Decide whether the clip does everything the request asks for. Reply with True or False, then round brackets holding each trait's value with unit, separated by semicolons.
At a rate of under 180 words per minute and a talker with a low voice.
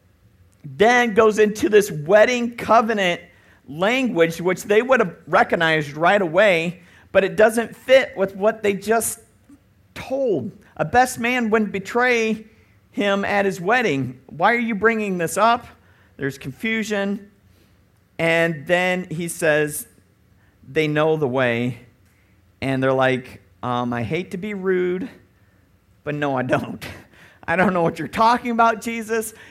False (140 wpm; 180 Hz)